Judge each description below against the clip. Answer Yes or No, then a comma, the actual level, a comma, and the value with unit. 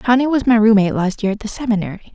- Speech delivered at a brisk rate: Yes, fast, 250 wpm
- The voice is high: Yes, high, 220 Hz